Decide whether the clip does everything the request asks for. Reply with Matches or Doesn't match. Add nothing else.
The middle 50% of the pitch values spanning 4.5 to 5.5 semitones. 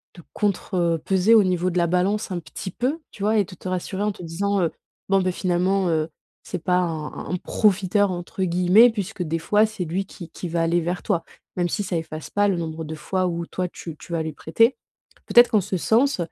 Doesn't match